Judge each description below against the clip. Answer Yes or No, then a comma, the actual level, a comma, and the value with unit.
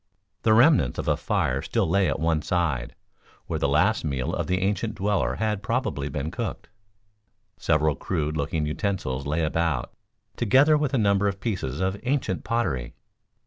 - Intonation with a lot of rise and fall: Yes, wide, 6.2 semitones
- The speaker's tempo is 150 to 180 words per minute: Yes, average, 165 wpm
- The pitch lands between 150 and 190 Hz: No, very low, 90 Hz